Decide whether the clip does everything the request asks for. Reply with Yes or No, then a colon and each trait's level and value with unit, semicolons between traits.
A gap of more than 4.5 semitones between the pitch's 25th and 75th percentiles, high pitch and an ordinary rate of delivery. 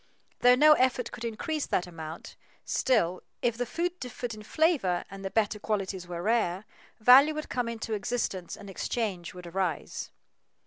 Yes: average, 5.2 semitones; high, 220 Hz; average, 165 wpm